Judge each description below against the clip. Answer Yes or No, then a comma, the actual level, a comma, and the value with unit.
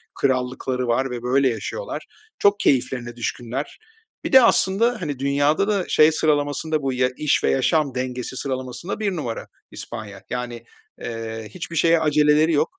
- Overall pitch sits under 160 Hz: Yes, low, 135 Hz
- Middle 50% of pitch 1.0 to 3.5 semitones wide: No, average, 4.0 semitones